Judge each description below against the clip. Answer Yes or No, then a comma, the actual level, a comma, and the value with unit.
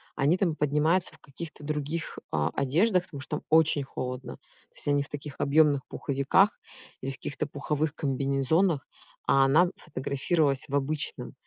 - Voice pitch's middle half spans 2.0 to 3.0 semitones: Yes, narrow, 2.6 semitones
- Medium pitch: Yes, medium, 145 Hz